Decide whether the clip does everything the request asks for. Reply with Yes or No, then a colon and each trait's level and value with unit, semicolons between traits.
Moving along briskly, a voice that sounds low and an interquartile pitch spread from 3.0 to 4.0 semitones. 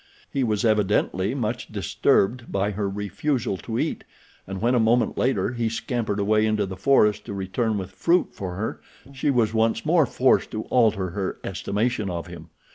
No: average, 180 wpm; low, 110 Hz; average, 3.5 semitones